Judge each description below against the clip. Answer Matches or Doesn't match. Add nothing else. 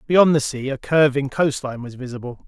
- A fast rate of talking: Doesn't match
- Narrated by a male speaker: Matches